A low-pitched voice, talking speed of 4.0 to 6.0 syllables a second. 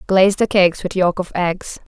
No: medium, 185 Hz; 5.5 syllables/s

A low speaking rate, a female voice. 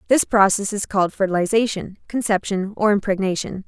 Yes: slow, 130 wpm; female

